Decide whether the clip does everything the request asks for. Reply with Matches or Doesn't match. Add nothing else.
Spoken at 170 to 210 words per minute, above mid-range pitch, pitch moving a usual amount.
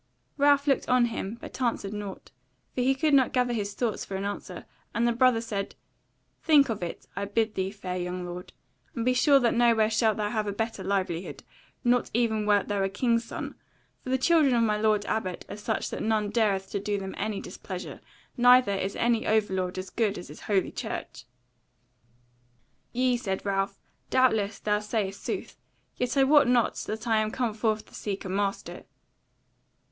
Matches